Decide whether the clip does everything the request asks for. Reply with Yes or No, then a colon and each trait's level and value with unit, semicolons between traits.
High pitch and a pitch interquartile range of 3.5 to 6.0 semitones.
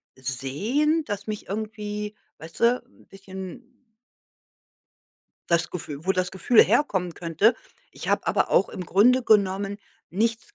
Yes: high, 205 Hz; average, 4.0 semitones